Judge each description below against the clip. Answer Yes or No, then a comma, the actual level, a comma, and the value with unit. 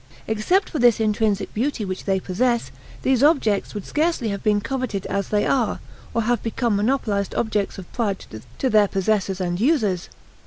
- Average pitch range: Yes, average, 3.6 semitones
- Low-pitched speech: No, high, 215 Hz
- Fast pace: No, average, 170 wpm